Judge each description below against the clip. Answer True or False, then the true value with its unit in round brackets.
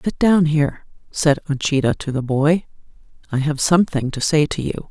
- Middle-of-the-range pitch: True (150 Hz)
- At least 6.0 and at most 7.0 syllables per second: False (5.3 syllables/s)